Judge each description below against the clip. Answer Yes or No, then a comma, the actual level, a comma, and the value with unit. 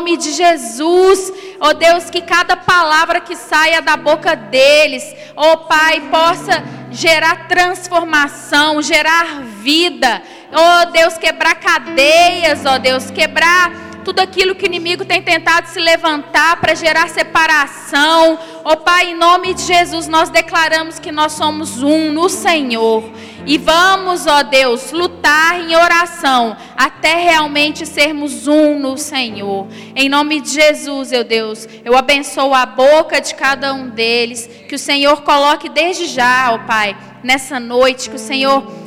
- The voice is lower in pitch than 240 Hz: No, very high, 310 Hz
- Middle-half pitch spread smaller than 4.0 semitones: Yes, average, 3.6 semitones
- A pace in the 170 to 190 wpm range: No, average, 155 wpm